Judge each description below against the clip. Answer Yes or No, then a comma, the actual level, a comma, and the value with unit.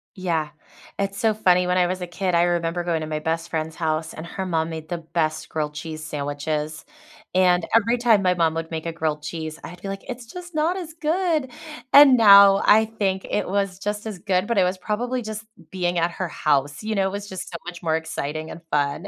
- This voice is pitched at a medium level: Yes, medium, 180 Hz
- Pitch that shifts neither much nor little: Yes, average, 4.4 semitones